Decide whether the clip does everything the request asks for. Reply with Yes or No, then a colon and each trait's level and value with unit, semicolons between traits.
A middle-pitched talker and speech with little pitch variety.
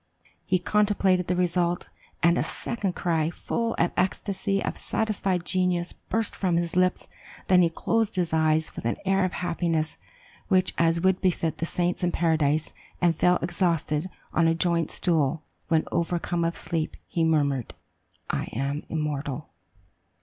Yes: medium, 170 Hz; narrow, 2.2 semitones